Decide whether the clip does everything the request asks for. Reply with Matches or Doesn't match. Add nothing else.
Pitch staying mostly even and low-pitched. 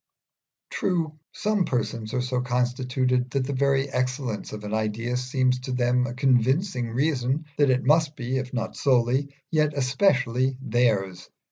Matches